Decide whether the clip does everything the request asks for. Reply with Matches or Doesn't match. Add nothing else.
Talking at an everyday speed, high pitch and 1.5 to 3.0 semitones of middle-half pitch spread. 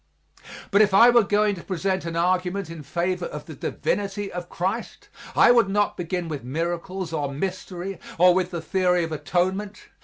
Doesn't match